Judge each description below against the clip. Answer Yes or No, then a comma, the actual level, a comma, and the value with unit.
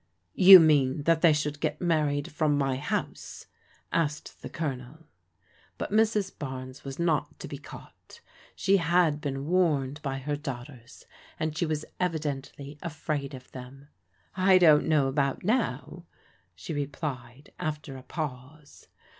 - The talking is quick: No, average, 145 wpm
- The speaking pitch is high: No, medium, 150 Hz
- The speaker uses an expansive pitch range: No, average, 3.0 semitones